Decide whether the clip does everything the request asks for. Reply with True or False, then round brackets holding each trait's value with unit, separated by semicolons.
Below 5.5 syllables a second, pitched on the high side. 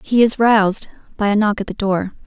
False (5.6 syllables/s; 210 Hz)